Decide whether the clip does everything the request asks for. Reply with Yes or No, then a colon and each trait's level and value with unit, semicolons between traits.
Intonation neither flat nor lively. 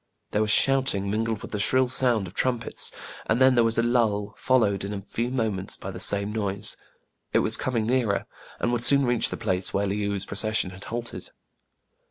Yes: average, 3.3 semitones